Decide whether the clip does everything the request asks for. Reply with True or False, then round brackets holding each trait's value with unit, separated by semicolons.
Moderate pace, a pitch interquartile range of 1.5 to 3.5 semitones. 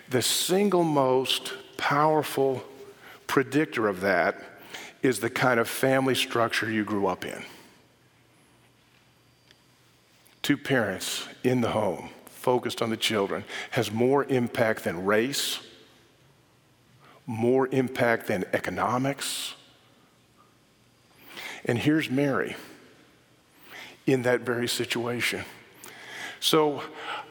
False (95 wpm; 2.8 semitones)